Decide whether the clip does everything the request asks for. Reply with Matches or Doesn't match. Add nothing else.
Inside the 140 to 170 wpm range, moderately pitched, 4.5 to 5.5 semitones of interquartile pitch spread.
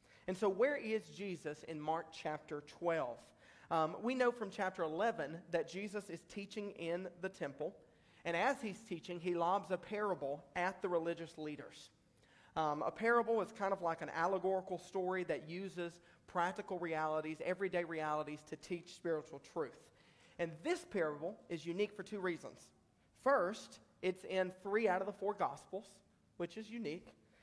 Doesn't match